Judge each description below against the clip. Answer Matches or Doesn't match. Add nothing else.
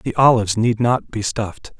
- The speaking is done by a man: Matches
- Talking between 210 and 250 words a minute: Doesn't match